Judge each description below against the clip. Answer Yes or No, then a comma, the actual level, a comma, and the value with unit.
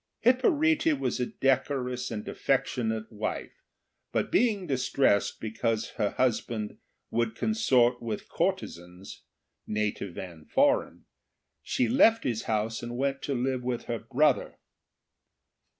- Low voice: Yes, low, 125 Hz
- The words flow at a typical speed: No, slow, 120 wpm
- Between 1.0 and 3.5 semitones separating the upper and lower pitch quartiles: No, average, 4.7 semitones